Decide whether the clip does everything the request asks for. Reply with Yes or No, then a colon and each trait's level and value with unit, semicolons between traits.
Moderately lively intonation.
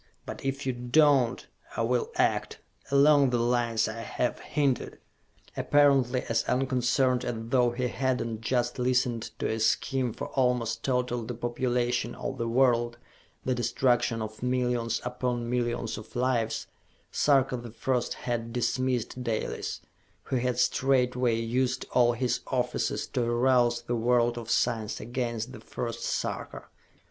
No: narrow, 1.4 semitones